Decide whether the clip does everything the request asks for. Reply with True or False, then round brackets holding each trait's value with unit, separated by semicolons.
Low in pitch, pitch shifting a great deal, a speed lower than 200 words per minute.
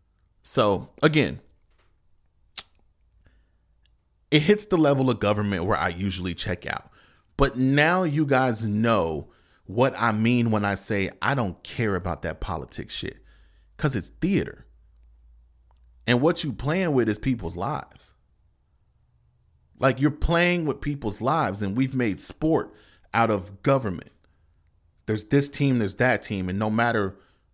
True (105 Hz; 7.3 semitones; 140 wpm)